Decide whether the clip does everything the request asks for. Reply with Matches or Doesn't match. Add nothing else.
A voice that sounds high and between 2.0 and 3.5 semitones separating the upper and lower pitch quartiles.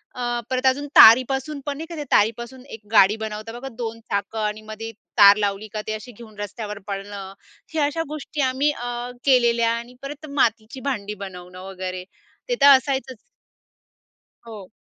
Doesn't match